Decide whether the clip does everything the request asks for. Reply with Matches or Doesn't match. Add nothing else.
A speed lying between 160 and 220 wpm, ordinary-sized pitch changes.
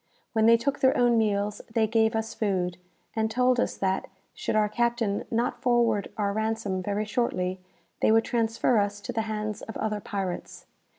Doesn't match